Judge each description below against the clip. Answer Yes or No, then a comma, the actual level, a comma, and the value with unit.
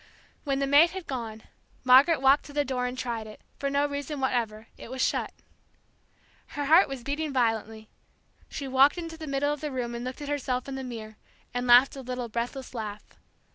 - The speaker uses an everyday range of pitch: Yes, average, 3.0 semitones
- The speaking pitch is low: No, very high, 265 Hz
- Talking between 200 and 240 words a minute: Yes, fast, 205 wpm